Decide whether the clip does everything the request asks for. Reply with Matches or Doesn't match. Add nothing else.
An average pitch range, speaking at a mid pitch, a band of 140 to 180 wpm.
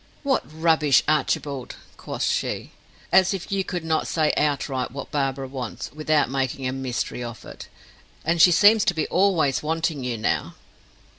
Matches